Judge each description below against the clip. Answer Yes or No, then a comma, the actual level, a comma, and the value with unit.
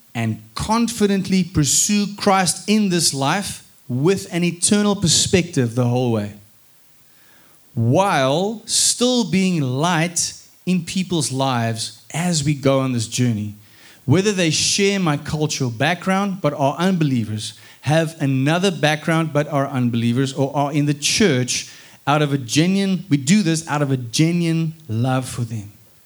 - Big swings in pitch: Yes, wide, 5.8 semitones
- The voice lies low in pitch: No, medium, 150 Hz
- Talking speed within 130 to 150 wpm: Yes, average, 140 wpm